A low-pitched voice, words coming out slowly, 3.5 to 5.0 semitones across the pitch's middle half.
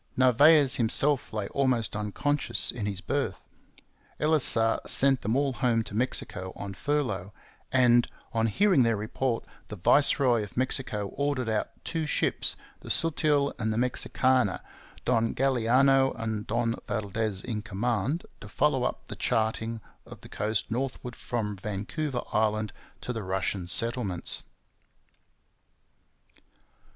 Yes: low, 115 Hz; slow, 130 wpm; average, 3.9 semitones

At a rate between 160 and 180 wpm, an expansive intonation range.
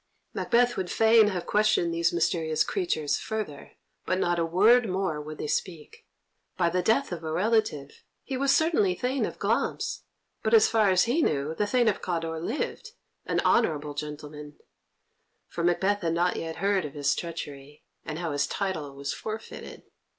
Yes: average, 170 wpm; wide, 5.8 semitones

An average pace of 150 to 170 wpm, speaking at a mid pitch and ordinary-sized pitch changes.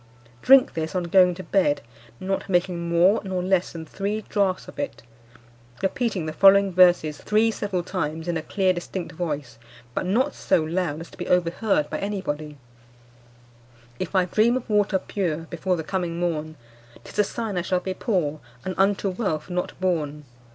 No: average, 180 wpm; medium, 180 Hz; average, 3.0 semitones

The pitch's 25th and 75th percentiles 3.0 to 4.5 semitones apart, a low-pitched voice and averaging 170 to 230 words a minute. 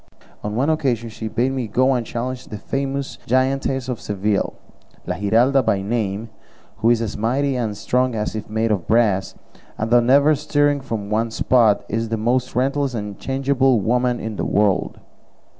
Yes: average, 3.5 semitones; low, 120 Hz; average, 175 wpm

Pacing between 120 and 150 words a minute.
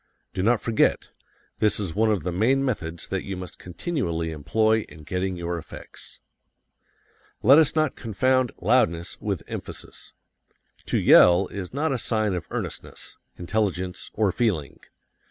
Yes: average, 145 wpm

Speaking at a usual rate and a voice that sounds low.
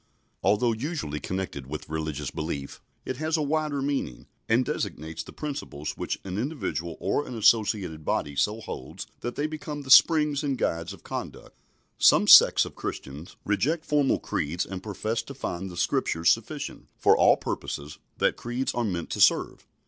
Yes: average, 170 wpm; low, 110 Hz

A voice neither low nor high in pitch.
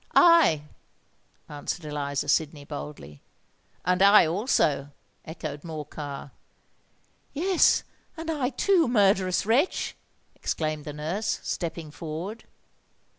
Yes: medium, 165 Hz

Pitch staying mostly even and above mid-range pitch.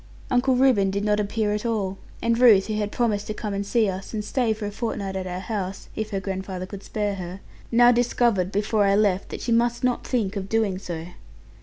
No: average, 3.0 semitones; high, 210 Hz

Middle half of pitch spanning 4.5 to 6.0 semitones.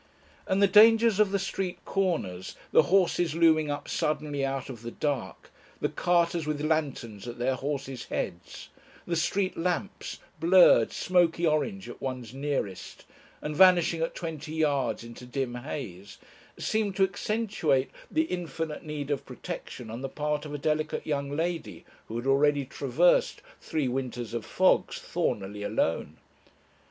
Yes: average, 5.0 semitones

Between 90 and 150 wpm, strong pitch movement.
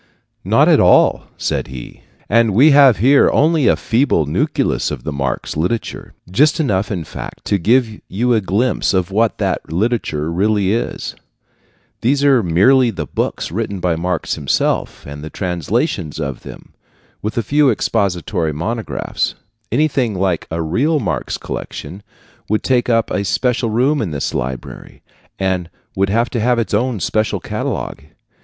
No: average, 160 wpm; wide, 6.0 semitones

